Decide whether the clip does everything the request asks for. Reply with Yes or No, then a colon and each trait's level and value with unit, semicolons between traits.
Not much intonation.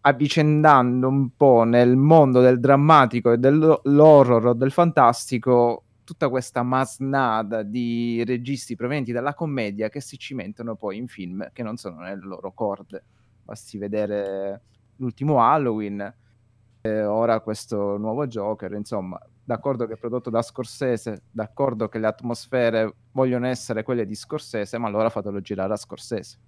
No: average, 3.0 semitones